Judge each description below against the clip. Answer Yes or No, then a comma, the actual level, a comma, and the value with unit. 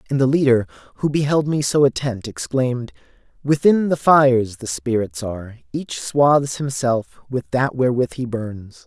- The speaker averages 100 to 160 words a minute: Yes, average, 155 wpm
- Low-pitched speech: Yes, low, 130 Hz